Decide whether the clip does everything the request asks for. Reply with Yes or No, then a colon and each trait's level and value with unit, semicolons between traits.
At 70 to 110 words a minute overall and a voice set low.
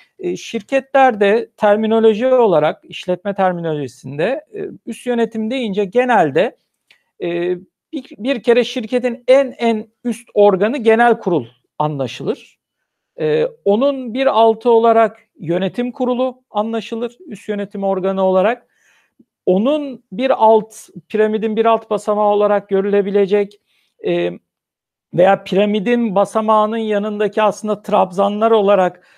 No: slow, 95 wpm; high, 220 Hz